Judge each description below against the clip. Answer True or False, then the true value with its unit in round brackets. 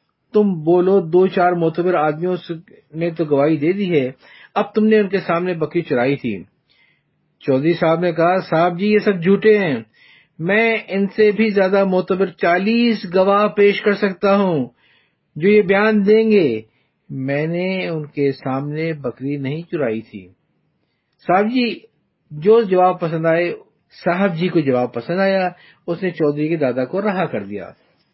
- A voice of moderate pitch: True (175 Hz)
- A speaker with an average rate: True (165 wpm)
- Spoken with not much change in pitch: False (4.5 semitones)